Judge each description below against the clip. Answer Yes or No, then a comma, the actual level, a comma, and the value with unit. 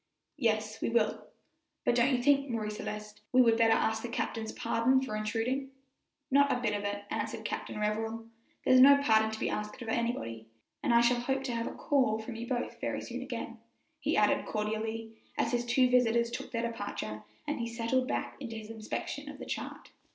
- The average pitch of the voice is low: No, high, 230 Hz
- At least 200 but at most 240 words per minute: Yes, fast, 205 wpm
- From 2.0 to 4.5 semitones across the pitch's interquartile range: Yes, narrow, 2.5 semitones